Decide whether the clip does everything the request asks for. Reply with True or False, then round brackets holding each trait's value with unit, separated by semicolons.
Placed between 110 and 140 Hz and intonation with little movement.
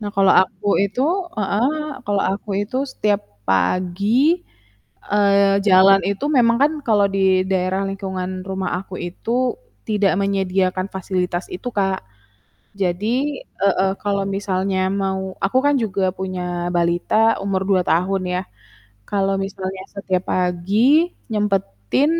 False (195 Hz; 1.5 semitones)